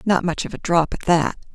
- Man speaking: No, female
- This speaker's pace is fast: Yes, fast, 270 wpm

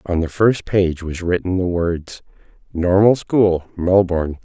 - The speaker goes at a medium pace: Yes, average, 150 wpm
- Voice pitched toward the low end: Yes, very low, 90 Hz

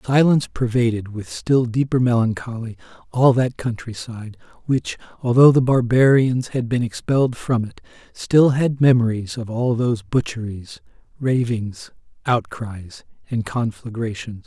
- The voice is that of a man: Yes, male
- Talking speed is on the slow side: Yes, slow, 120 wpm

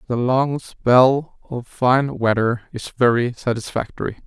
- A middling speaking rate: No, slow, 125 wpm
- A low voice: Yes, low, 125 Hz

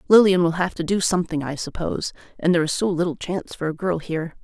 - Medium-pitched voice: Yes, medium, 170 Hz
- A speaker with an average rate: No, fast, 245 wpm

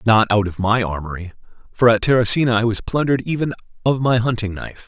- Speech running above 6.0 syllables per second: Yes, 6.5 syllables/s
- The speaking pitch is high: No, low, 115 Hz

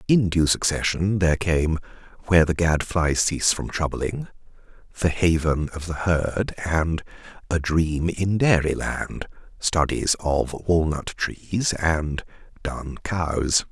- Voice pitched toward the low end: Yes, very low, 85 Hz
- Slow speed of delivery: Yes, slow, 125 wpm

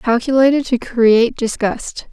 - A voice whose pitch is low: No, high, 240 Hz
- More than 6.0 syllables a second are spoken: No, 4.5 syllables/s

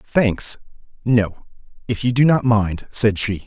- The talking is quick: No, average, 140 wpm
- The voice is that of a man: Yes, male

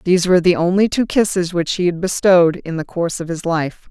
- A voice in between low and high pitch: Yes, medium, 175 Hz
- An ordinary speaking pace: No, fast, 245 wpm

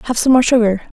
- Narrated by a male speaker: No, female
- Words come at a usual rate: No, fast, 245 wpm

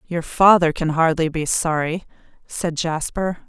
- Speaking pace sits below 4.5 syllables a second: Yes, 4.1 syllables/s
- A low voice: No, medium, 165 Hz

